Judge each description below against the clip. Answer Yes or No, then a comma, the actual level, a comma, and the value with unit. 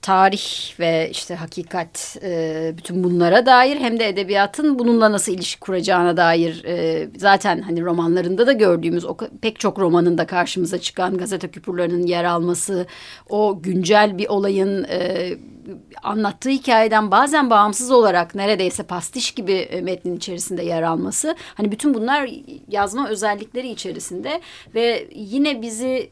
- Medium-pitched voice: No, high, 195 Hz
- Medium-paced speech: Yes, average, 125 wpm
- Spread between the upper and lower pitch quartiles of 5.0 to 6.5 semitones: No, average, 4.3 semitones